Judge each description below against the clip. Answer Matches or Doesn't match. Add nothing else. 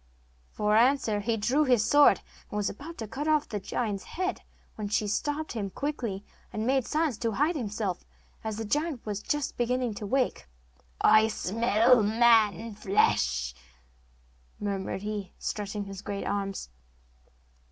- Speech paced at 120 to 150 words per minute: Doesn't match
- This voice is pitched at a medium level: Doesn't match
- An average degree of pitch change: Matches